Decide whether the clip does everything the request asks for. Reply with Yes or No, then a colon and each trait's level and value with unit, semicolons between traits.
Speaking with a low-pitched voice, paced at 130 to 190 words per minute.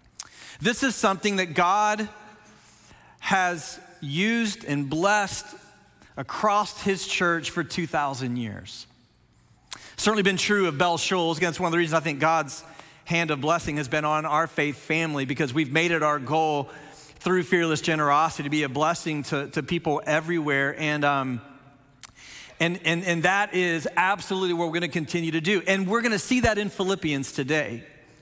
No: medium, 165 Hz; average, 170 wpm